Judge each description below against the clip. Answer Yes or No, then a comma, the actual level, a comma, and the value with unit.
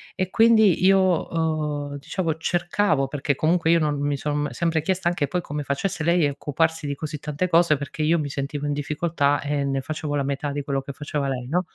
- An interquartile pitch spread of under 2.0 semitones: No, average, 2.9 semitones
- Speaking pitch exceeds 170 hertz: No, medium, 150 Hz